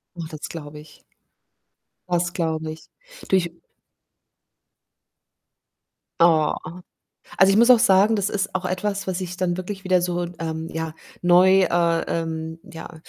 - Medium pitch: Yes, medium, 175 Hz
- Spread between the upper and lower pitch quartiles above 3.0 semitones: No, average, 2.7 semitones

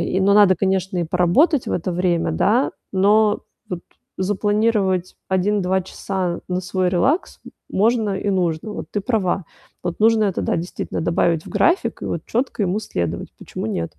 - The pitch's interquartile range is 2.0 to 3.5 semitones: Yes, average, 2.9 semitones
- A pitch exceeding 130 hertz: Yes, high, 190 Hz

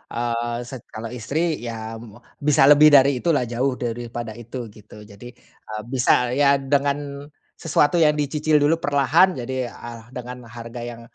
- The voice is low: Yes, low, 125 Hz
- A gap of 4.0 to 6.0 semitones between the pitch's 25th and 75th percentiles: No, average, 3.5 semitones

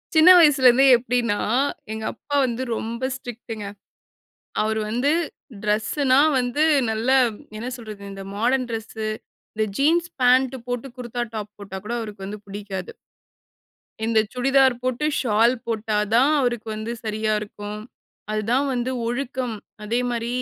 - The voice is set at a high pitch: Yes, high, 235 Hz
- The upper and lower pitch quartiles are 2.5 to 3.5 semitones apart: Yes, average, 3.0 semitones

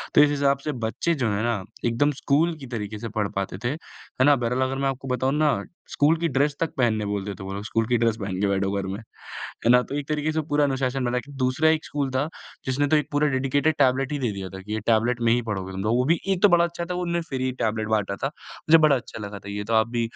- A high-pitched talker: No, low, 130 Hz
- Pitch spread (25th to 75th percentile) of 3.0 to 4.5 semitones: No, average, 5.0 semitones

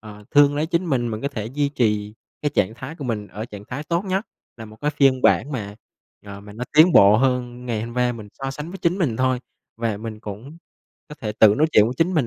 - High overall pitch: No, low, 125 Hz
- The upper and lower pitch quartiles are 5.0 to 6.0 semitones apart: Yes, average, 5.3 semitones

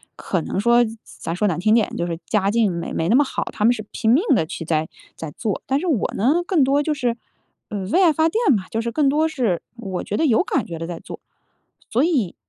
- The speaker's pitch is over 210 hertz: Yes, high, 230 Hz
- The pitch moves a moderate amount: No, wide, 7.2 semitones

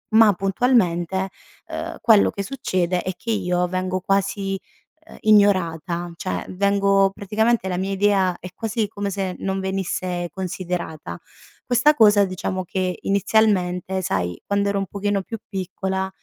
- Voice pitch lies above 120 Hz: Yes, high, 190 Hz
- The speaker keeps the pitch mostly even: Yes, narrow, 1.8 semitones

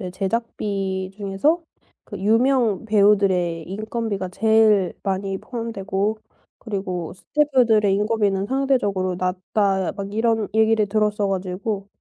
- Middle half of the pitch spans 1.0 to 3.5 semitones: Yes, narrow, 2.5 semitones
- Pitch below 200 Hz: No, high, 205 Hz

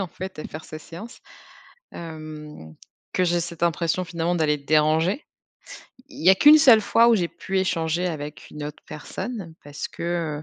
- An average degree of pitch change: Yes, average, 3.2 semitones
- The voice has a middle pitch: Yes, medium, 170 Hz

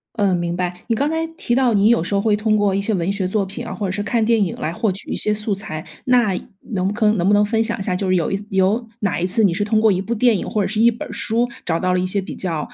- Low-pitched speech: No, high, 205 Hz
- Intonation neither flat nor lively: Yes, average, 3.1 semitones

